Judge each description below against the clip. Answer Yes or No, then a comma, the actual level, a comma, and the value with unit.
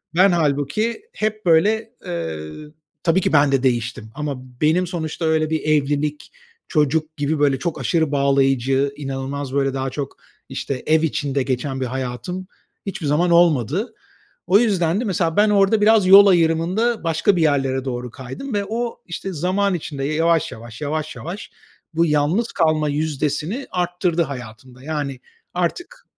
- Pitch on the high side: No, medium, 155 Hz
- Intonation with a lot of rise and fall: No, average, 4.6 semitones